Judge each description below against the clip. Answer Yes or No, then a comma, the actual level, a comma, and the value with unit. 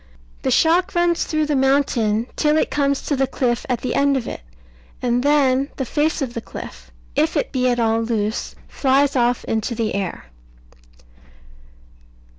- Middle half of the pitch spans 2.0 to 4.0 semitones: Yes, average, 3.7 semitones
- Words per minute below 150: No, average, 170 wpm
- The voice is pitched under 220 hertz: No, very high, 260 Hz